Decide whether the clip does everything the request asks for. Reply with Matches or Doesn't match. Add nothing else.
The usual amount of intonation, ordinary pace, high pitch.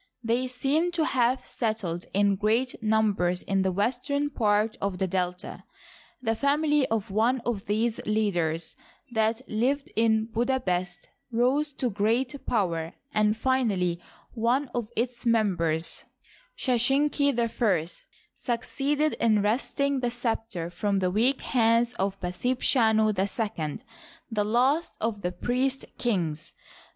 Doesn't match